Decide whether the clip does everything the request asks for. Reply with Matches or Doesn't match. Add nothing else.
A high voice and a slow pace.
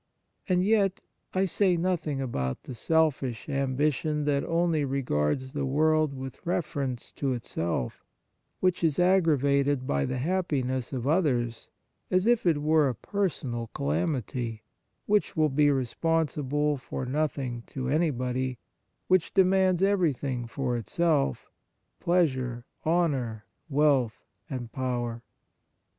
Doesn't match